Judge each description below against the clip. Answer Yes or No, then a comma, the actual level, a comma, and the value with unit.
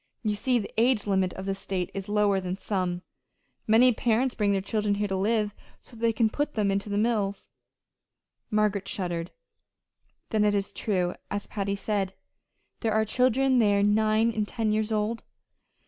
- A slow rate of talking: No, average, 180 wpm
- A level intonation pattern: Yes, narrow, 2.0 semitones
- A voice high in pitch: Yes, high, 210 Hz